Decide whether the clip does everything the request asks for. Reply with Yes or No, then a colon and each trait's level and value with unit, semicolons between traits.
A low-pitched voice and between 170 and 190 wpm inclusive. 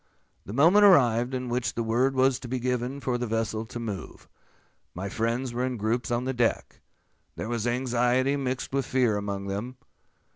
Yes: low, 120 Hz; average, 185 wpm